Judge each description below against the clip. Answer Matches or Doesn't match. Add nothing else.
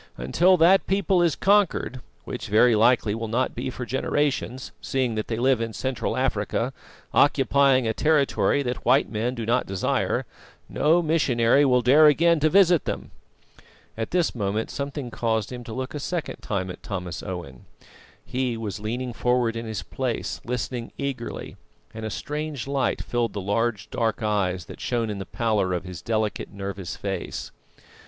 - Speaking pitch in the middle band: Doesn't match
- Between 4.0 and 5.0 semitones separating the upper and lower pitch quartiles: Matches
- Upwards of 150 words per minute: Matches